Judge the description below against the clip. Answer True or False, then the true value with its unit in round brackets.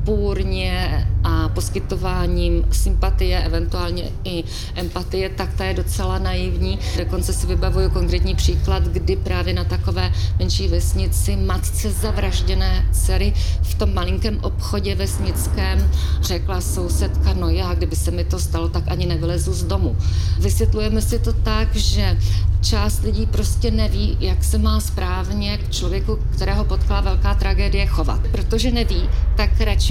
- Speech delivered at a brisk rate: False (140 wpm)